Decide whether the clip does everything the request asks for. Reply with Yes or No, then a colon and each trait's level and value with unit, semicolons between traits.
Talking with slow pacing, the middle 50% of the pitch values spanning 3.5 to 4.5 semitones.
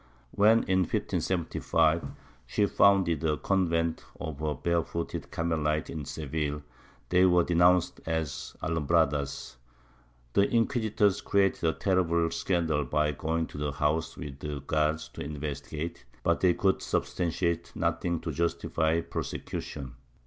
No: slow, 130 wpm; narrow, 2.6 semitones